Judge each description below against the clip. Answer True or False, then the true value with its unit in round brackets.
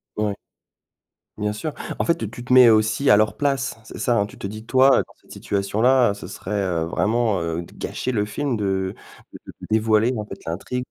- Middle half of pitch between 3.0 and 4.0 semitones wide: True (3.5 semitones)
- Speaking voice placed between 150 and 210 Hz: False (110 Hz)